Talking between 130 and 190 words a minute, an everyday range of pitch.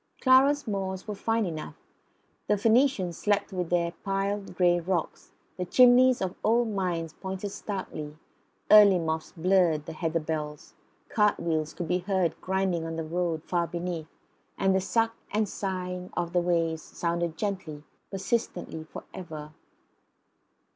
Yes: average, 145 wpm; average, 3.4 semitones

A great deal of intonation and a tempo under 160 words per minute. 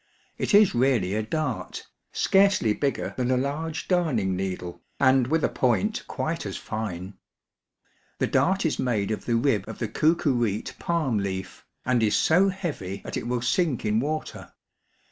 No: wide, 6.9 semitones; average, 165 wpm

